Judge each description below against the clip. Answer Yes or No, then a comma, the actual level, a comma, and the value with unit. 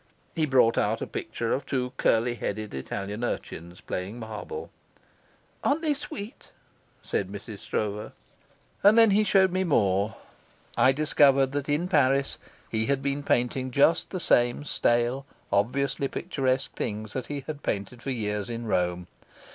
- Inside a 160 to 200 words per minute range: No, average, 150 wpm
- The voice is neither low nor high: No, low, 130 Hz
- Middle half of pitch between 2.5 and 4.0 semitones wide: No, average, 5.0 semitones